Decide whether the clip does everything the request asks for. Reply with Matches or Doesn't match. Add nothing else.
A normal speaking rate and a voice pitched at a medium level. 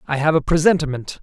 Matches